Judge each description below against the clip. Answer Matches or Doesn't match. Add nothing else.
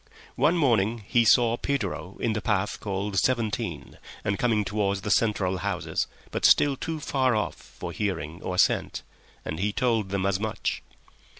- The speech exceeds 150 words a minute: Matches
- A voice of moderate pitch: Doesn't match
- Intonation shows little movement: Doesn't match